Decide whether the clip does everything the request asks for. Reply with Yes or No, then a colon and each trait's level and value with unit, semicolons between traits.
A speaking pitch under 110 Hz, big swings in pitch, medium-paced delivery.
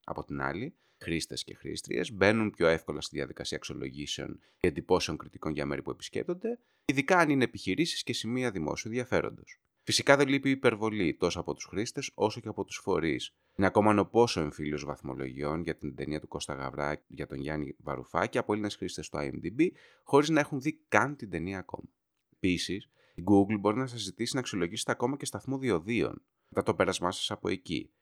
No: low, 100 Hz; wide, 8.7 semitones; fast, 190 wpm